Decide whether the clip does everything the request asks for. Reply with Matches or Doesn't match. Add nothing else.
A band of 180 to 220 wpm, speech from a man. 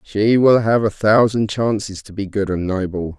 Matches